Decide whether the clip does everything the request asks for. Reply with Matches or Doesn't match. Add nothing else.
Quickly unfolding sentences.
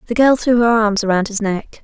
Matches